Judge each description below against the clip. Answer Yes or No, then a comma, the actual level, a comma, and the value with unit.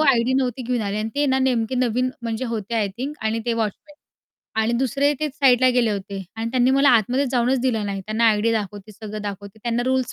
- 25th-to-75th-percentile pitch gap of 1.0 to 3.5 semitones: Yes, average, 3.2 semitones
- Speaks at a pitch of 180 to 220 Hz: No, high, 235 Hz